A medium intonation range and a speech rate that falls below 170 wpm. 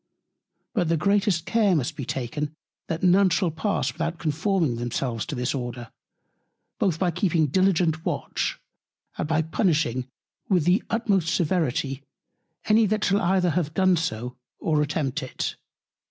Yes: average, 4.7 semitones; average, 140 wpm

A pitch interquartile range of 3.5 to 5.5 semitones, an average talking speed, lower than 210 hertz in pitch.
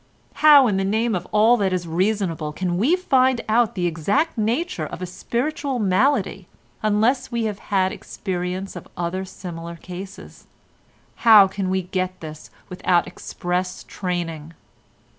Yes: average, 4.3 semitones; average, 145 wpm; high, 190 Hz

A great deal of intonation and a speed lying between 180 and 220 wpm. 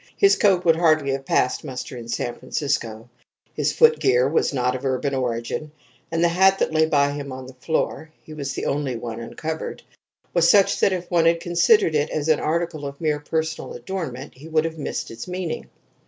No: average, 4.3 semitones; average, 200 wpm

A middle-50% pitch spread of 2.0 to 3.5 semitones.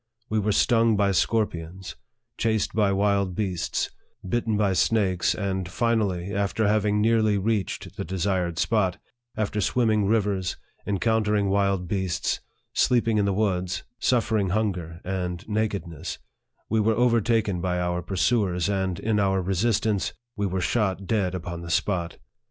Yes: average, 2.9 semitones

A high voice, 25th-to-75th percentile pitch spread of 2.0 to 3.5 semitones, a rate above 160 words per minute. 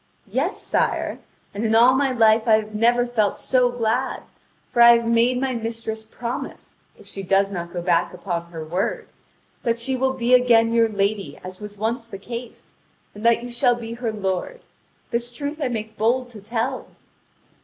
Yes: high, 230 Hz; average, 2.7 semitones; average, 185 wpm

